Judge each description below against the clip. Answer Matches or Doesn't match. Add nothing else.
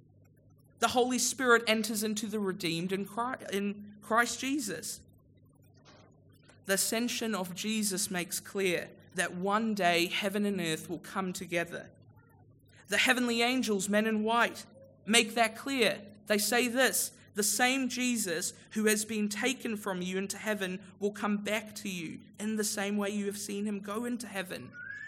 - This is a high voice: Matches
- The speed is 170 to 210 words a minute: Doesn't match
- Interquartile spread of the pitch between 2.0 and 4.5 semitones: Matches